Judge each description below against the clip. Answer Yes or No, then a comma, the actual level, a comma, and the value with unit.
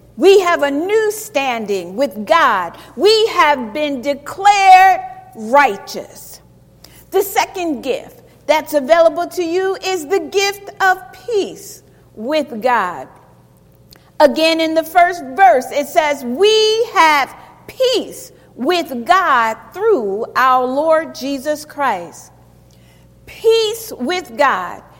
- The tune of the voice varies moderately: No, wide, 5.7 semitones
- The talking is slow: Yes, slow, 110 wpm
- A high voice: Yes, very high, 330 Hz